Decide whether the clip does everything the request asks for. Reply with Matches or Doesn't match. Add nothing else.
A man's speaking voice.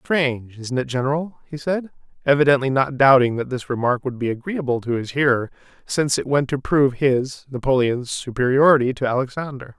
Matches